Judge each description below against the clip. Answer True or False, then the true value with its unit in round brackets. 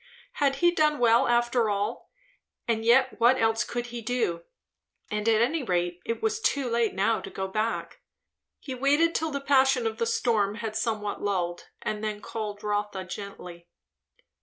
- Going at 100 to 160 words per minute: False (170 wpm)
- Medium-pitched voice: False (225 Hz)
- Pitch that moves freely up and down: False (3.7 semitones)